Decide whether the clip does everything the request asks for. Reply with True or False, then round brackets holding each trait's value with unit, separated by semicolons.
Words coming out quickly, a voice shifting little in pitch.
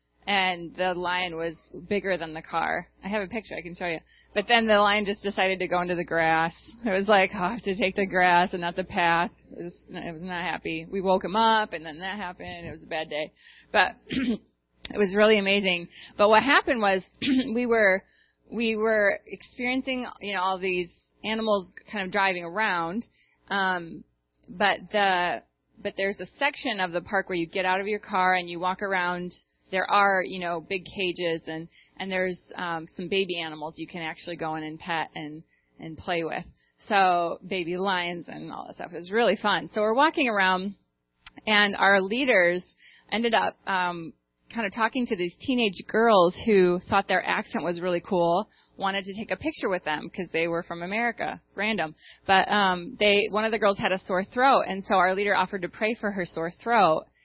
False (210 wpm; 3.1 semitones)